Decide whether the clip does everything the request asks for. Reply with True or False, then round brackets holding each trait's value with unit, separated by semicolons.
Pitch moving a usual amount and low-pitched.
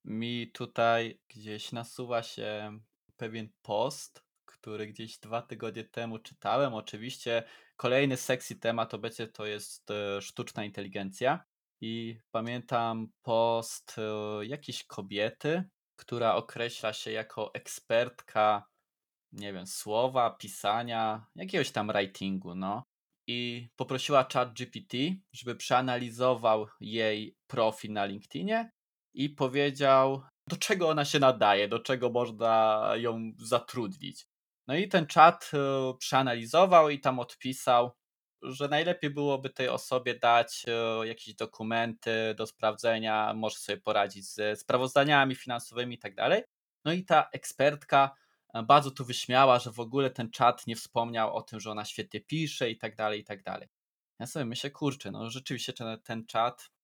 True (3.2 semitones; 115 Hz)